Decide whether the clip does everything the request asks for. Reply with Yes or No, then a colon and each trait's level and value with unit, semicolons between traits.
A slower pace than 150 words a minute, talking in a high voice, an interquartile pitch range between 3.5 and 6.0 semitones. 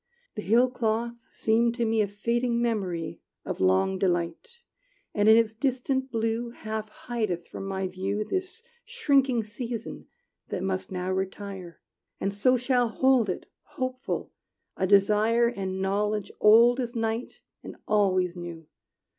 Yes: average, 140 wpm; high, 220 Hz; average, 3.9 semitones